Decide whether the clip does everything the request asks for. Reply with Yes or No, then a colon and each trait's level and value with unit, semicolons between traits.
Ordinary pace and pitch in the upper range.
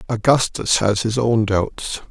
No: average, 145 wpm; low, 110 Hz